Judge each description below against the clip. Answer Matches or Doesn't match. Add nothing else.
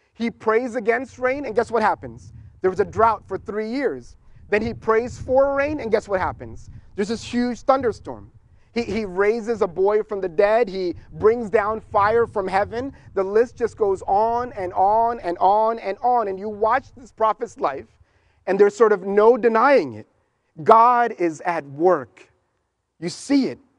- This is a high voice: Matches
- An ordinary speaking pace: Matches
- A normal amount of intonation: Matches